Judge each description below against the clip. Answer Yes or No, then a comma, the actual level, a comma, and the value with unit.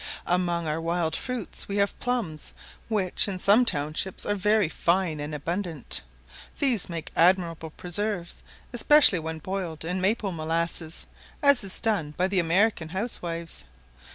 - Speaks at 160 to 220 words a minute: No, average, 140 wpm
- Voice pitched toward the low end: No, medium, 180 Hz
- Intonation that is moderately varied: Yes, average, 3.8 semitones